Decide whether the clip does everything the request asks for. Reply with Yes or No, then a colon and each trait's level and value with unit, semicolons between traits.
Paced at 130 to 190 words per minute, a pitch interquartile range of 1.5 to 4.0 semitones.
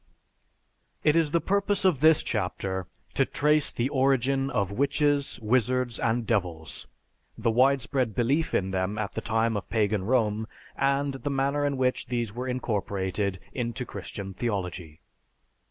No: average, 145 wpm; average, 5.2 semitones